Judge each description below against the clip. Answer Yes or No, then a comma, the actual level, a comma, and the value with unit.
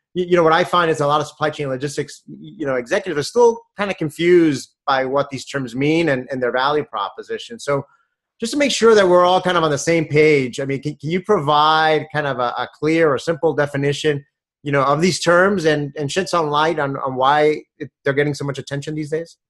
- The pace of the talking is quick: Yes, fast, 245 wpm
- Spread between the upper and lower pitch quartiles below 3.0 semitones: No, average, 3.7 semitones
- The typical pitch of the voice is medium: Yes, medium, 150 Hz